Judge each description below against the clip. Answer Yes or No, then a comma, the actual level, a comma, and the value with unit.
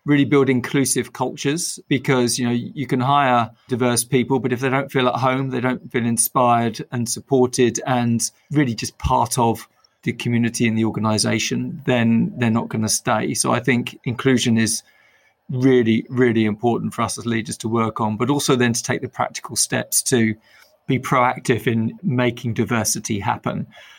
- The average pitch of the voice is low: Yes, low, 120 Hz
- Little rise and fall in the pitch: Yes, narrow, 2.2 semitones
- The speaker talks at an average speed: Yes, average, 180 wpm